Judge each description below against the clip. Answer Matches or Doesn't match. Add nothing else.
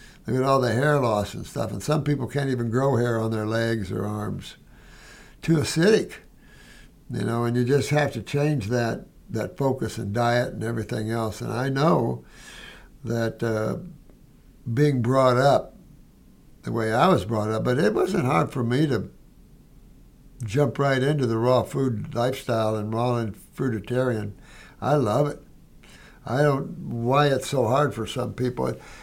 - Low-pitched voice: Matches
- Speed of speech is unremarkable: Matches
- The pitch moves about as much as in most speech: Matches